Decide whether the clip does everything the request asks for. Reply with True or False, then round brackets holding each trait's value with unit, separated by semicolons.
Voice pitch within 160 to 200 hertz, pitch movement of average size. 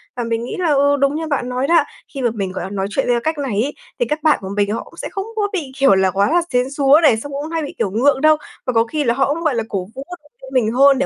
False (270 Hz; 4.7 semitones)